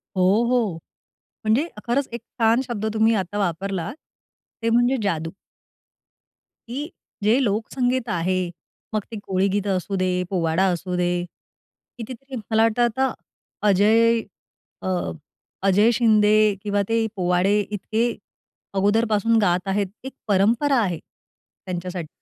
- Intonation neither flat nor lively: Yes, average, 3.6 semitones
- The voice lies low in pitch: No, high, 210 Hz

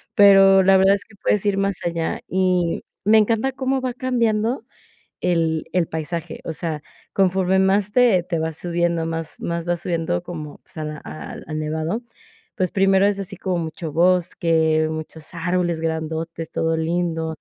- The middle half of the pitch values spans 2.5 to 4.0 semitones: Yes, average, 3.2 semitones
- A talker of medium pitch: Yes, medium, 175 Hz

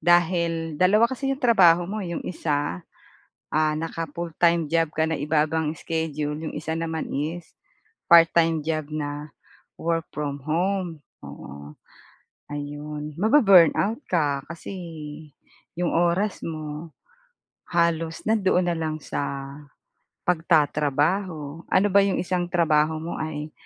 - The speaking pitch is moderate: Yes, medium, 165 Hz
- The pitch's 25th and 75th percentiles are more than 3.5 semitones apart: No, narrow, 2.5 semitones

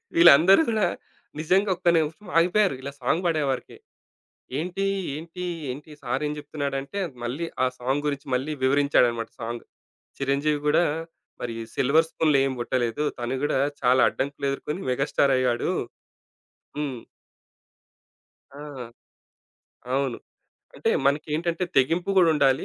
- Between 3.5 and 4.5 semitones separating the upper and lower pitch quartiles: Yes, average, 3.8 semitones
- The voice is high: No, medium, 145 Hz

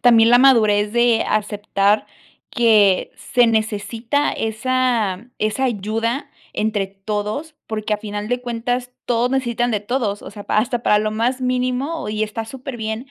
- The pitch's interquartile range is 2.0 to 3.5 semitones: Yes, average, 2.7 semitones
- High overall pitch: Yes, high, 225 Hz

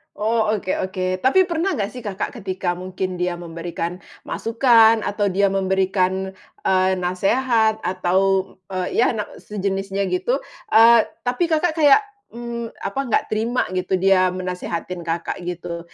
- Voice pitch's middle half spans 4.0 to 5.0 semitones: No, average, 3.6 semitones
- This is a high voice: Yes, high, 195 Hz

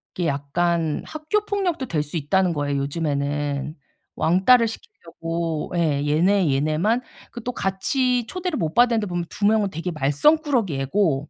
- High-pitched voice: No, medium, 175 Hz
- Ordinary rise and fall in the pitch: No, wide, 7.6 semitones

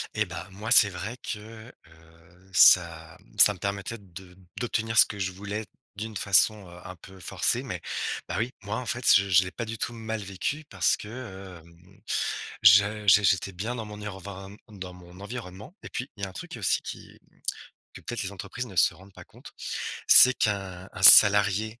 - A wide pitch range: No, average, 2.8 semitones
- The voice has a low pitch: Yes, low, 100 Hz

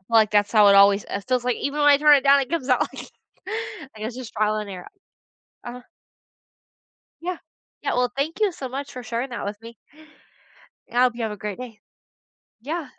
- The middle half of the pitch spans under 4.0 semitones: No, average, 4.8 semitones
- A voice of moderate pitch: No, very high, 250 Hz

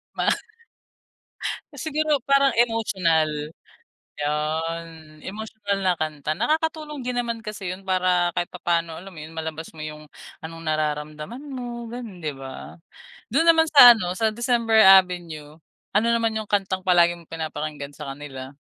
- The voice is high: No, medium, 180 Hz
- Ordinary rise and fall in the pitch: No, wide, 6.9 semitones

